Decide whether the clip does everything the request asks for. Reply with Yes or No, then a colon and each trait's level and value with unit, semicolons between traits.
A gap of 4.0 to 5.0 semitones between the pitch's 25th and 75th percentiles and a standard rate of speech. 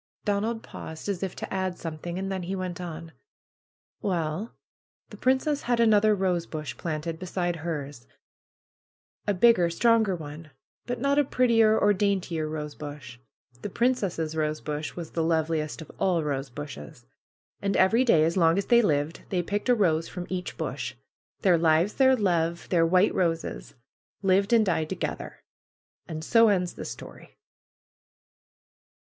Yes: average, 4.4 semitones; average, 155 wpm